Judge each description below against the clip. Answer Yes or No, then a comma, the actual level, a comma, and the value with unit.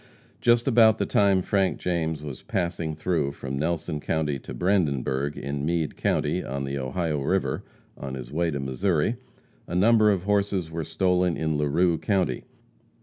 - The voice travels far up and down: No, average, 4.7 semitones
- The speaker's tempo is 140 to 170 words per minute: Yes, average, 160 wpm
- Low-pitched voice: Yes, very low, 80 Hz